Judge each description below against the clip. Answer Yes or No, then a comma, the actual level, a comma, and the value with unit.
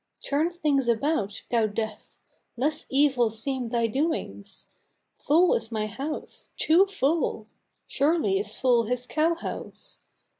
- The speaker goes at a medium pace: No, slow, 125 wpm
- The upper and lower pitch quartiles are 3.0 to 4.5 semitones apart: No, wide, 5.5 semitones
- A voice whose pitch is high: Yes, very high, 270 Hz